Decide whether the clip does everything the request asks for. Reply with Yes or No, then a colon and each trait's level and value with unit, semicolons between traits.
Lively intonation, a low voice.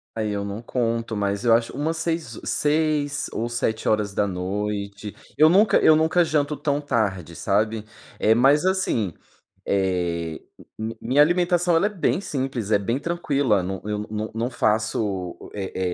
Yes: wide, 6.7 semitones; low, 115 Hz